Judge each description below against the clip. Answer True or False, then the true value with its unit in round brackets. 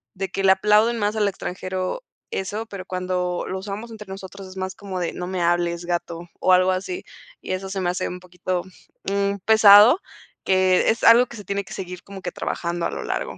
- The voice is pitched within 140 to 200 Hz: True (190 Hz)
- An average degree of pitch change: False (1.9 semitones)